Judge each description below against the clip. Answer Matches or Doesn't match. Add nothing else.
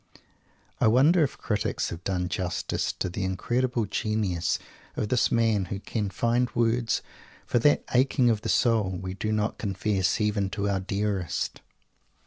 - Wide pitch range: Doesn't match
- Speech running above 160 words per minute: Doesn't match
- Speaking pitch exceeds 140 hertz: Doesn't match